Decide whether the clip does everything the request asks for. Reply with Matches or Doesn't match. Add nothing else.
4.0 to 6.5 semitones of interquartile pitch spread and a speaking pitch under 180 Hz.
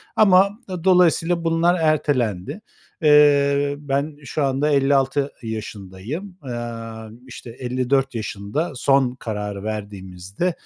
Matches